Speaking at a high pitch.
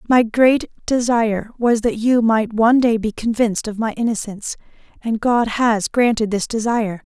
Yes: high, 225 Hz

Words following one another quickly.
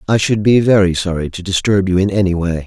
Yes: fast, 245 wpm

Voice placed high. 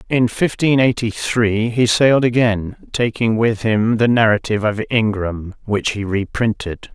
No: low, 110 Hz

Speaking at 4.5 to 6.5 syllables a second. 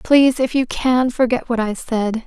Yes: 4.6 syllables/s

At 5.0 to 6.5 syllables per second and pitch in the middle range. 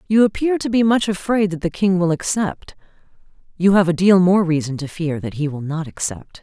Yes: 5.3 syllables/s; medium, 180 Hz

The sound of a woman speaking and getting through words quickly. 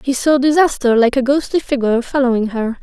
No: female; average, 190 wpm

